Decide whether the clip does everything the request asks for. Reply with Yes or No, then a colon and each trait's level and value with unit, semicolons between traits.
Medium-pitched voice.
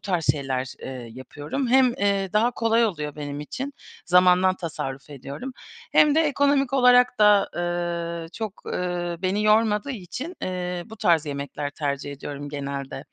Yes: medium, 180 Hz